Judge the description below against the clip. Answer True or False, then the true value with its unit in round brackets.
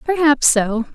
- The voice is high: True (270 Hz)